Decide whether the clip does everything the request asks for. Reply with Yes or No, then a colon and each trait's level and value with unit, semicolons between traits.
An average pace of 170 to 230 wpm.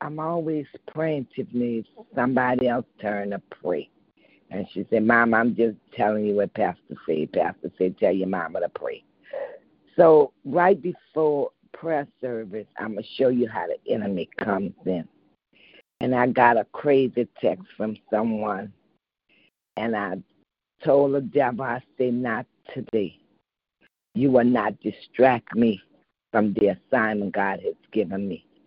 No: average, 145 wpm